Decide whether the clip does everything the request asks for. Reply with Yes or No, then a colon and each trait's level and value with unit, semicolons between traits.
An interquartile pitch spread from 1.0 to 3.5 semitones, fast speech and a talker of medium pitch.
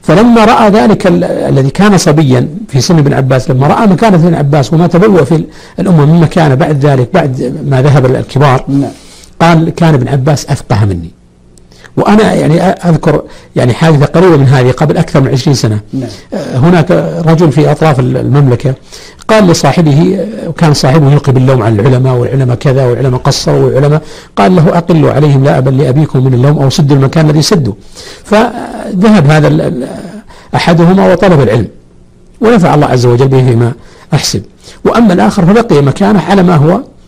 No: average, 4.7 semitones; fast, 155 wpm; medium, 150 Hz